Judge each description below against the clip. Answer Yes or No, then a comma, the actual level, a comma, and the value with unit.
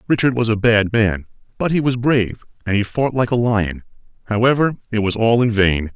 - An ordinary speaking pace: No, fast, 210 wpm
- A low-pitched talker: Yes, low, 115 Hz